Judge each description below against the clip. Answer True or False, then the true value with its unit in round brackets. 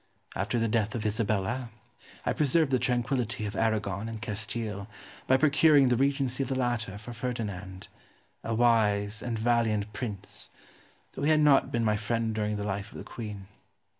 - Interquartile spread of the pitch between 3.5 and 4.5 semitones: False (3.0 semitones)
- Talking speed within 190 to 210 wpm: False (170 wpm)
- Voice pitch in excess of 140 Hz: False (115 Hz)